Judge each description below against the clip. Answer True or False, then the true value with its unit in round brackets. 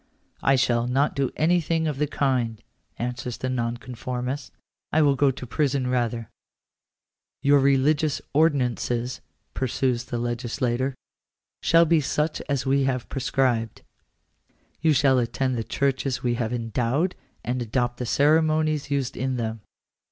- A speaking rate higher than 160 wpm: False (145 wpm)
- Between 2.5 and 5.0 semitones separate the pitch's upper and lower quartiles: True (2.8 semitones)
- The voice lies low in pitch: True (130 Hz)